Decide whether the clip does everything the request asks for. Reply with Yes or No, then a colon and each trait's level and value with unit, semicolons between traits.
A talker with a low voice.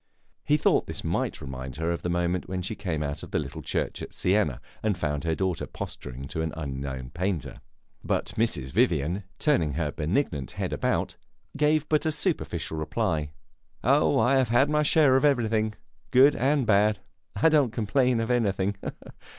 Yes: low, 100 Hz